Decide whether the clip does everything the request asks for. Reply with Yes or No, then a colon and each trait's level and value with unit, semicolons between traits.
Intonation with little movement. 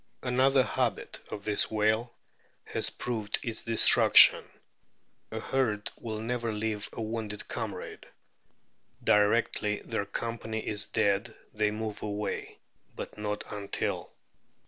Yes: narrow, 1.7 semitones